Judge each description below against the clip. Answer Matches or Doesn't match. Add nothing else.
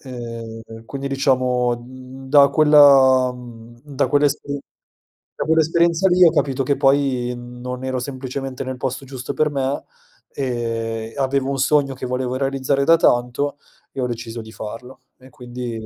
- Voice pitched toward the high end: Doesn't match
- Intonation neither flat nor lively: Doesn't match